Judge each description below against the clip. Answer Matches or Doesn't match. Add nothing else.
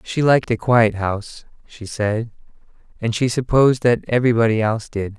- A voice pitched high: Doesn't match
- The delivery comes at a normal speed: Matches